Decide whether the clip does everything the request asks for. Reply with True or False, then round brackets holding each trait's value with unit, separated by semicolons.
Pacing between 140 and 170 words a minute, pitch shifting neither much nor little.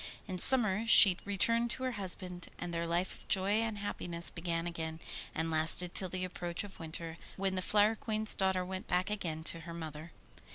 False (195 wpm; 3.3 semitones)